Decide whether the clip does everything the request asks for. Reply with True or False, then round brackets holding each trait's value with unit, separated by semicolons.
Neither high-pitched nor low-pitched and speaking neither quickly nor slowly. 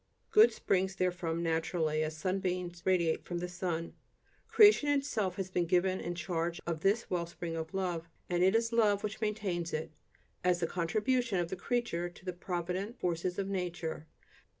True (180 Hz; 170 wpm)